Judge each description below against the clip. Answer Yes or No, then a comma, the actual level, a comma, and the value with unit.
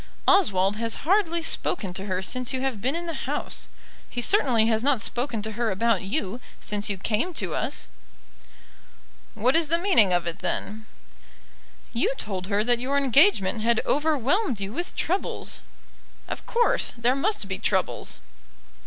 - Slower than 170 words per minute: Yes, average, 160 wpm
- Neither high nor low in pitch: No, high, 240 Hz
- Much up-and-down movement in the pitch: Yes, wide, 6.7 semitones